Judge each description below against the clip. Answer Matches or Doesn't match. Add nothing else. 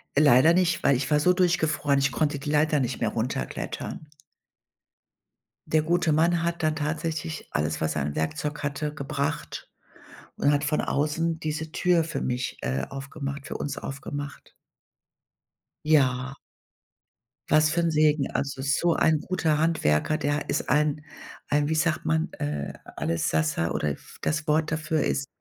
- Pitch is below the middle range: Doesn't match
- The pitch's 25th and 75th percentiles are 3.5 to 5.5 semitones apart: Doesn't match